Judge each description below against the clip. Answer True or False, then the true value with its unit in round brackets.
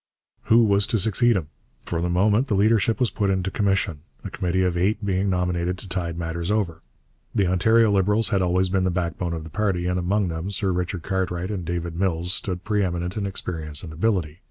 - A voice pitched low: True (95 Hz)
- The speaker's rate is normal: False (210 wpm)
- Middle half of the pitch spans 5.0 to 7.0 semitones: False (2.6 semitones)